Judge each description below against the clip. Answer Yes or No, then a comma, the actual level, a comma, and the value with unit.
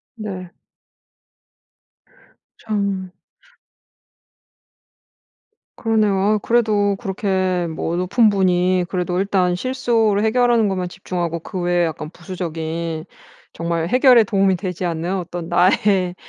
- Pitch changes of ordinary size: Yes, average, 3.0 semitones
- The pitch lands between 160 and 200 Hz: Yes, medium, 185 Hz